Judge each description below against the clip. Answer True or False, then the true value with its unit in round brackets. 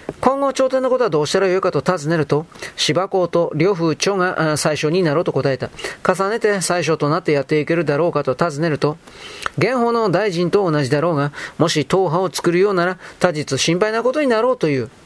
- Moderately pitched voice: True (175 Hz)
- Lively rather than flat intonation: False (4.6 semitones)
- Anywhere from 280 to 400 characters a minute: True (395 characters per minute)